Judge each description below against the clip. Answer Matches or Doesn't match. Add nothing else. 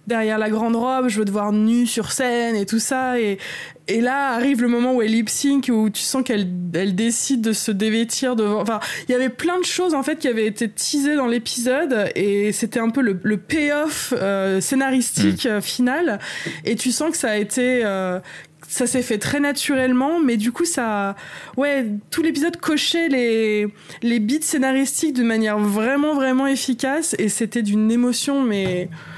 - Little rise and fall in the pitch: Doesn't match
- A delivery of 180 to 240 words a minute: Matches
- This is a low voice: Doesn't match